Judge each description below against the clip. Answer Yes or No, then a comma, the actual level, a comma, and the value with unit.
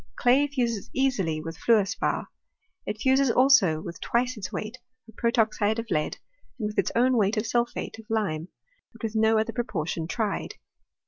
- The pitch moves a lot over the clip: No, average, 3.3 semitones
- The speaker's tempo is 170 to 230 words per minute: Yes, average, 175 wpm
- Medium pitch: No, high, 225 Hz